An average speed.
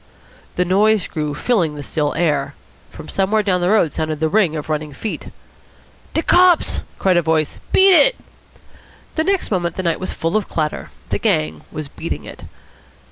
Yes: average, 175 wpm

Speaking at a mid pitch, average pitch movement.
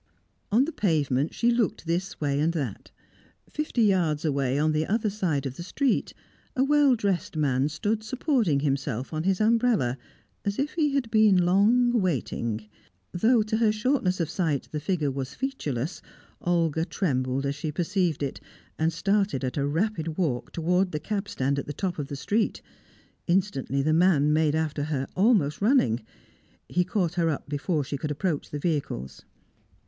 No: medium, 165 Hz; wide, 6.5 semitones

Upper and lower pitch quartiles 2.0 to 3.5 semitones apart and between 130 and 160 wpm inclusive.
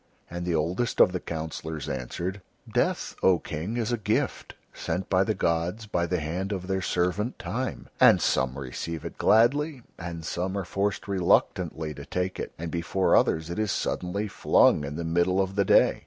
No: average, 3.2 semitones; average, 185 wpm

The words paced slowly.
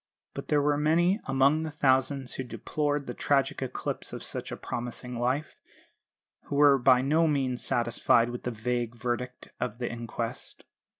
No: average, 165 wpm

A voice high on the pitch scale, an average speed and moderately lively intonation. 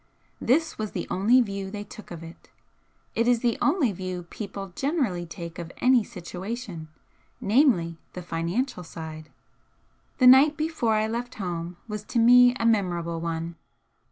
No: high, 200 Hz; average, 155 wpm; wide, 6.1 semitones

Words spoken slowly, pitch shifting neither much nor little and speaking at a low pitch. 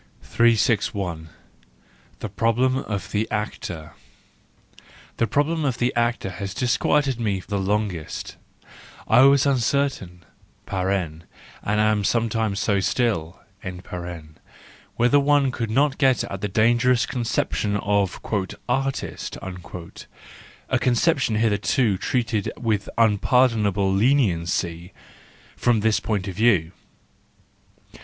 Yes: slow, 105 wpm; average, 4.2 semitones; low, 110 Hz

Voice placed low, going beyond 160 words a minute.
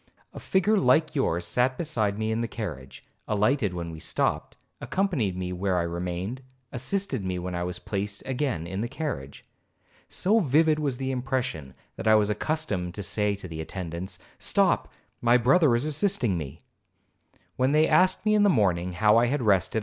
Yes: low, 110 Hz; average, 180 wpm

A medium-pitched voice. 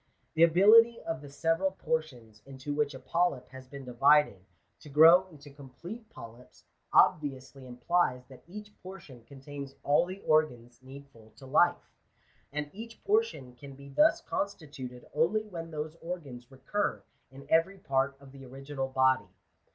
Yes: medium, 145 Hz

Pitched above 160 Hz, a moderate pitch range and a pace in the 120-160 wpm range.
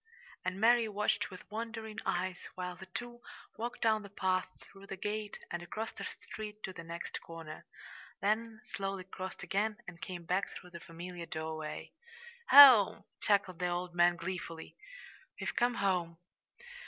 Yes: high, 190 Hz; average, 3.4 semitones; average, 155 wpm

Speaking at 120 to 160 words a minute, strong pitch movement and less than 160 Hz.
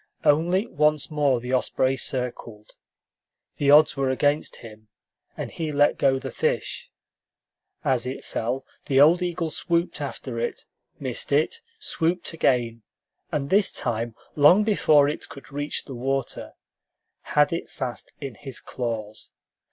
No: average, 140 wpm; average, 3.9 semitones; medium, 140 Hz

